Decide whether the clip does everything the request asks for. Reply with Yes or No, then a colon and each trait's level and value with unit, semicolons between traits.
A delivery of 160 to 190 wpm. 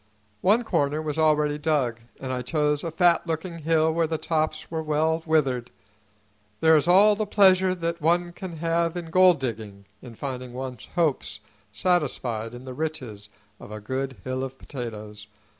Yes: average, 170 wpm